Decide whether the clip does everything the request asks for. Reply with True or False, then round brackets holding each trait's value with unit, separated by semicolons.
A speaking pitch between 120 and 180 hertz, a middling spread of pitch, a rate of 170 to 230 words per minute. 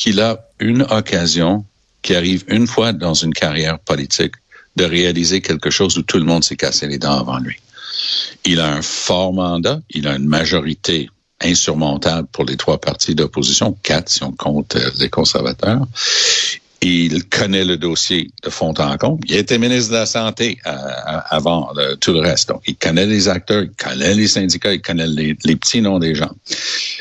False (85 Hz; 5.0 semitones; 180 wpm)